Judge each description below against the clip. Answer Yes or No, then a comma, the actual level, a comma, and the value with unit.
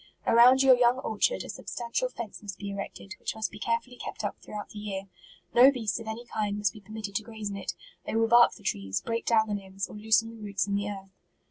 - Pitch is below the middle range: No, high, 215 Hz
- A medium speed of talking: No, fast, 250 wpm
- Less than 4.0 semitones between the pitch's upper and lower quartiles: Yes, narrow, 2.5 semitones